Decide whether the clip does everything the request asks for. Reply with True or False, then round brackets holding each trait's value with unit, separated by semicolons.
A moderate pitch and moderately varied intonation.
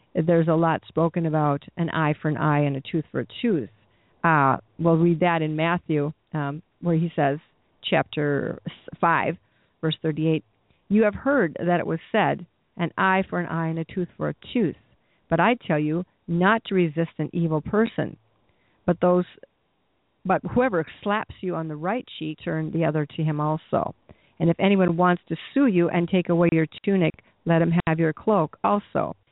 False (165 Hz; 2.3 semitones)